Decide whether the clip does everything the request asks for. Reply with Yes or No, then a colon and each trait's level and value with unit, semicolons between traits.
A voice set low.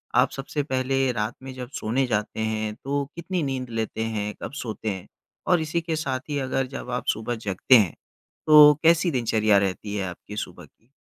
Yes: low, 125 Hz